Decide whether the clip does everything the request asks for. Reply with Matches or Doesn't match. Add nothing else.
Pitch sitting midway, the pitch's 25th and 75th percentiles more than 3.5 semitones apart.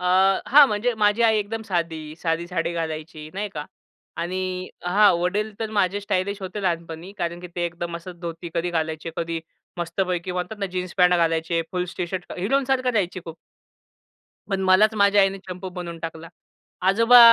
Doesn't match